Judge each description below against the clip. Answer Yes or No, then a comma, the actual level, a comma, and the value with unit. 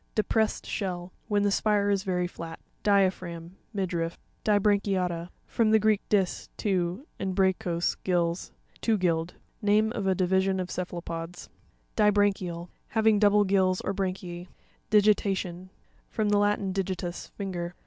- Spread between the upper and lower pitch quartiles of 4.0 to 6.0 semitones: No, narrow, 2.6 semitones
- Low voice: No, high, 190 Hz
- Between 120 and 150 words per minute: Yes, average, 145 wpm